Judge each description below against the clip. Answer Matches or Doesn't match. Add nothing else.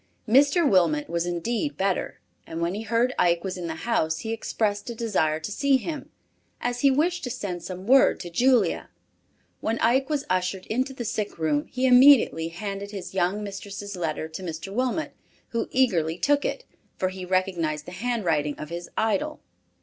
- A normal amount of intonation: Doesn't match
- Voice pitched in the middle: Doesn't match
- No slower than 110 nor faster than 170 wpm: Doesn't match